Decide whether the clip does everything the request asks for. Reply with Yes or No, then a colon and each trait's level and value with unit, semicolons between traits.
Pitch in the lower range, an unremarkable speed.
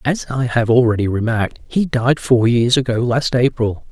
Yes: low, 120 Hz; average, 185 wpm